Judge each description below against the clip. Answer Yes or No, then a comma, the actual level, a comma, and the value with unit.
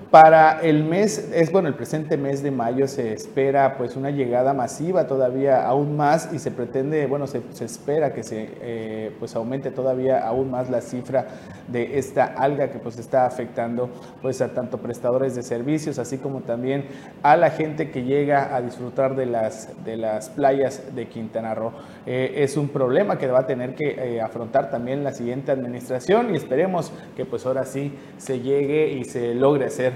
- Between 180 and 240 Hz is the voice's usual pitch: No, low, 130 Hz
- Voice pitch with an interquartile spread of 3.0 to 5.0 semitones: No, narrow, 2.6 semitones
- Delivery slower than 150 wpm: No, fast, 190 wpm